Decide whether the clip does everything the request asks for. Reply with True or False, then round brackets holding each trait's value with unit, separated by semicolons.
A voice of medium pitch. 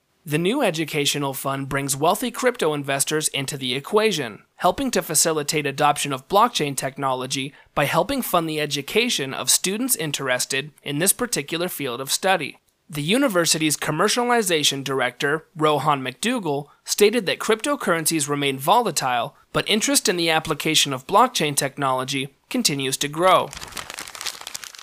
True (155 Hz)